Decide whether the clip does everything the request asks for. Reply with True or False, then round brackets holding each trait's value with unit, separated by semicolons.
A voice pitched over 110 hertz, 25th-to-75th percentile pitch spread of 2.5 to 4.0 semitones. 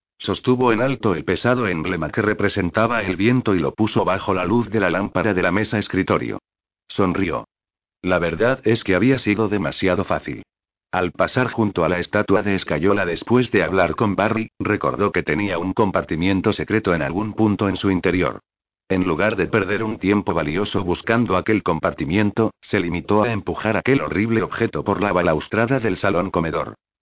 False (100 Hz; 3.3 semitones)